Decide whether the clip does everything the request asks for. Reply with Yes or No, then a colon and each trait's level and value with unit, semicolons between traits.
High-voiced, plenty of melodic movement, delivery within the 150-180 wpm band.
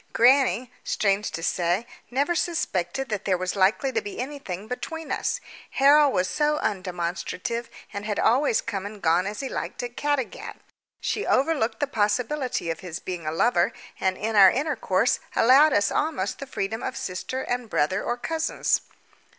Yes: high, 225 Hz; wide, 6.4 semitones; average, 165 wpm